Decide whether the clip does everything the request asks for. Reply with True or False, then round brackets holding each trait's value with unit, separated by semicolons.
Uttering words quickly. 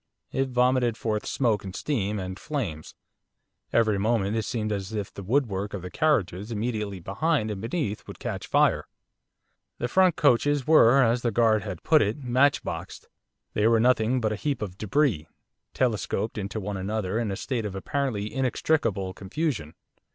False (165 wpm)